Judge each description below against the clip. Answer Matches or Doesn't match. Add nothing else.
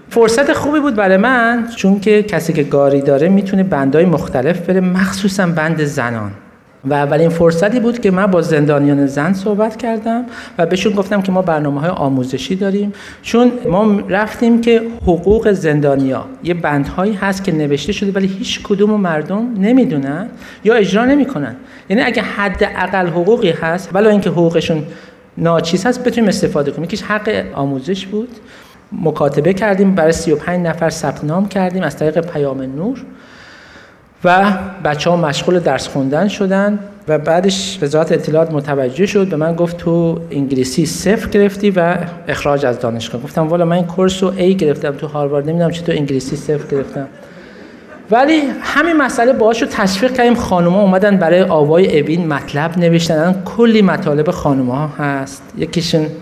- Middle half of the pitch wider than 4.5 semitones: Matches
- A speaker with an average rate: Doesn't match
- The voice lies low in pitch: Doesn't match